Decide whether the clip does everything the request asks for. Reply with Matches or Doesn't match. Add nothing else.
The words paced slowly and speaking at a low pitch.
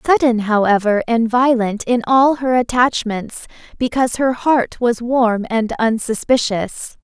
Doesn't match